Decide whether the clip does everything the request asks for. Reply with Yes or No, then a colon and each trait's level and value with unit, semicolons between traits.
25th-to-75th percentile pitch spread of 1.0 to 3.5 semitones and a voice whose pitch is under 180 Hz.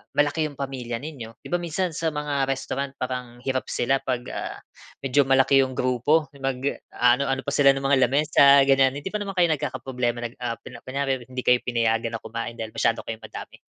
Yes: narrow, 2.5 semitones; low, 135 Hz